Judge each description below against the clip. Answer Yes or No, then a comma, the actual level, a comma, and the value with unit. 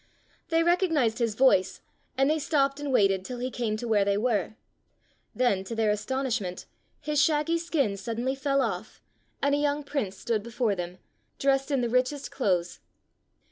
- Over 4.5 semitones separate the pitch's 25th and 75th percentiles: Yes, average, 5.1 semitones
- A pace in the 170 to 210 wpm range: Yes, average, 175 wpm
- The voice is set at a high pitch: Yes, very high, 250 Hz